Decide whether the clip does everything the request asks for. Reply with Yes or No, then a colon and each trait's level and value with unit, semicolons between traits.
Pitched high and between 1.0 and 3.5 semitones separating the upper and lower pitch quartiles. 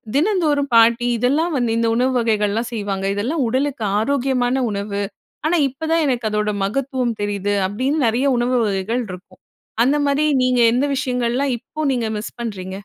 No: high, 245 Hz; average, 4.4 semitones